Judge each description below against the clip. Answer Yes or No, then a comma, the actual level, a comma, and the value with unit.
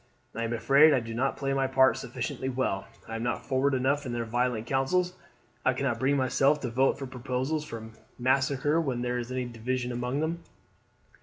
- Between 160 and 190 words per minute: No, average, 200 wpm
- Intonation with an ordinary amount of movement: No, narrow, 2.1 semitones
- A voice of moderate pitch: No, low, 130 Hz